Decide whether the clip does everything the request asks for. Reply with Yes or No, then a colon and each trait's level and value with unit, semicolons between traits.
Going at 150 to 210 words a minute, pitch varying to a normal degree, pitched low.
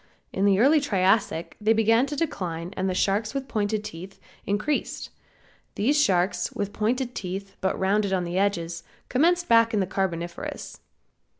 No: average, 160 wpm; average, 3.5 semitones; high, 200 Hz